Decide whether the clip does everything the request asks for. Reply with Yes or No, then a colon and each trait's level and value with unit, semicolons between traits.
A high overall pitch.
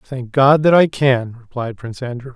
No: low, 130 Hz